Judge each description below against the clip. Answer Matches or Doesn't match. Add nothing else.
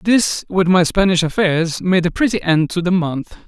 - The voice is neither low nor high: Matches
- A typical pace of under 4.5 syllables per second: Doesn't match